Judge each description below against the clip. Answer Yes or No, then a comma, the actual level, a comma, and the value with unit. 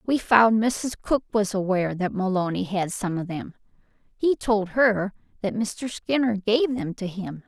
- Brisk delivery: No, average, 170 wpm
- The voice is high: Yes, high, 210 Hz